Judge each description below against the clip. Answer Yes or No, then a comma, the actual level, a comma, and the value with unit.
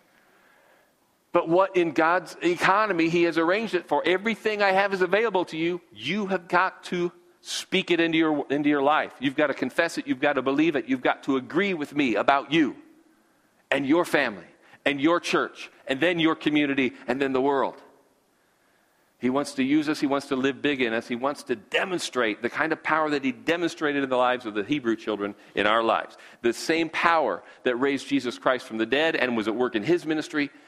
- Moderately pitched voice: Yes, medium, 155 Hz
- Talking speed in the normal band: No, fast, 215 wpm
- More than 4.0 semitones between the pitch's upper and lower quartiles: Yes, average, 4.8 semitones